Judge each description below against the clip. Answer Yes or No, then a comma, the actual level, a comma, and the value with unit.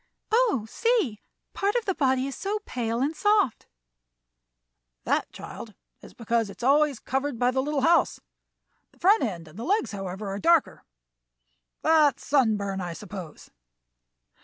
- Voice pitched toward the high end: Yes, very high, 265 Hz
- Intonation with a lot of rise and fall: Yes, wide, 7.7 semitones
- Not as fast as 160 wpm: Yes, average, 150 wpm